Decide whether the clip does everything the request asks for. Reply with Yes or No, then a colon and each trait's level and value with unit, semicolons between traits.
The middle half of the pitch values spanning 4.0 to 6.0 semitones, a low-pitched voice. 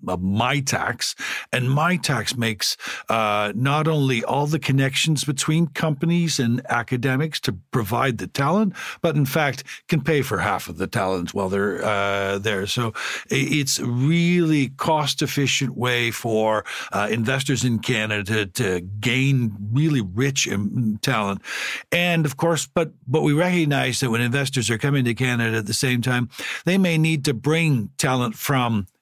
Yes: average, 5.1 semitones; low, 130 Hz